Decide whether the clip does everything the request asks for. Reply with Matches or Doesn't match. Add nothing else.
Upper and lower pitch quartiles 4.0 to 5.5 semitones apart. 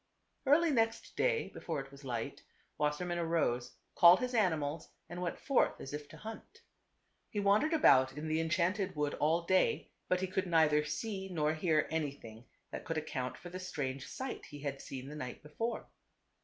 Matches